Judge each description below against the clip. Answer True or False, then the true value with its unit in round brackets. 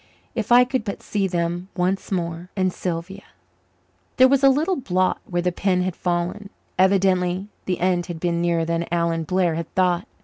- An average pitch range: False (2.3 semitones)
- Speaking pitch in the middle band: True (180 Hz)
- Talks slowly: False (180 wpm)